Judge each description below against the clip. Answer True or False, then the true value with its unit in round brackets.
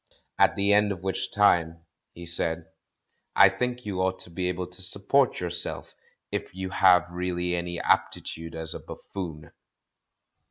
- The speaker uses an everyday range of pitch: False (2.2 semitones)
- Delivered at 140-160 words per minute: True (155 wpm)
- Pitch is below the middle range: True (90 Hz)